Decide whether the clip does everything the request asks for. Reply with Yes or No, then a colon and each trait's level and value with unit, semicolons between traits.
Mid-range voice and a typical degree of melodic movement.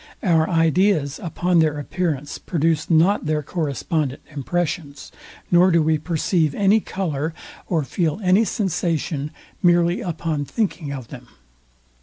Yes: medium, 165 Hz; average, 3.2 semitones